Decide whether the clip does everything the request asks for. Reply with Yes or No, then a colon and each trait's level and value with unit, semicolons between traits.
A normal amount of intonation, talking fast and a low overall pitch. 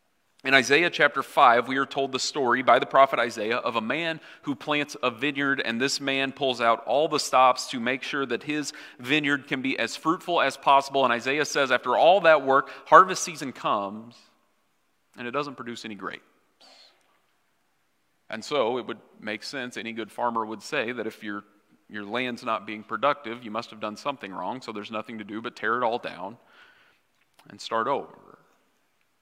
No: average, 3.9 semitones; average, 195 wpm; low, 130 Hz